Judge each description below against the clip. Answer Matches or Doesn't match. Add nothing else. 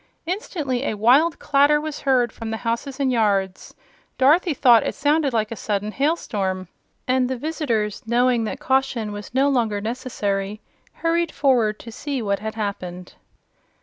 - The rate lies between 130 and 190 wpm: Matches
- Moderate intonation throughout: Matches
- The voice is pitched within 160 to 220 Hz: Doesn't match